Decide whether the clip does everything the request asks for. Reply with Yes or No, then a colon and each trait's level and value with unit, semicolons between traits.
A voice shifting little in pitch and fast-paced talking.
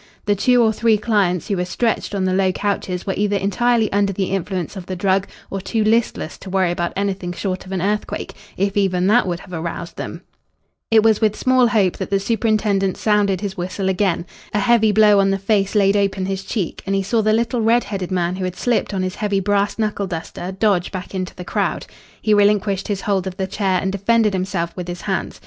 Yes: narrow, 2.2 semitones; fast, 225 wpm